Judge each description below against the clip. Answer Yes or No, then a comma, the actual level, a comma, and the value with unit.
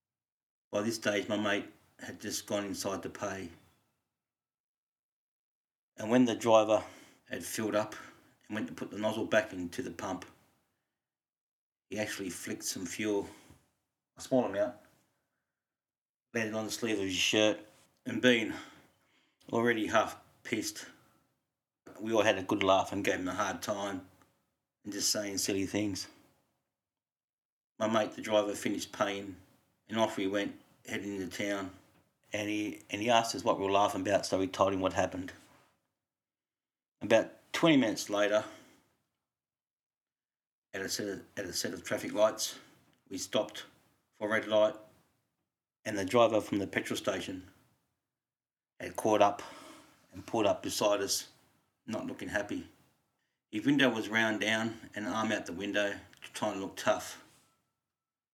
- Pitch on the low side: Yes, low, 105 Hz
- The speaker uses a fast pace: No, average, 155 wpm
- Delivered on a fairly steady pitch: Yes, narrow, 2.1 semitones